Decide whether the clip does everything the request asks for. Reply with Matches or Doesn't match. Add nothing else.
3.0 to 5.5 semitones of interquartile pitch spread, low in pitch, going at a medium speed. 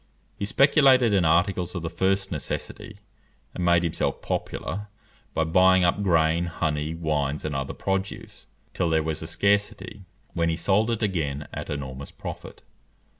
Matches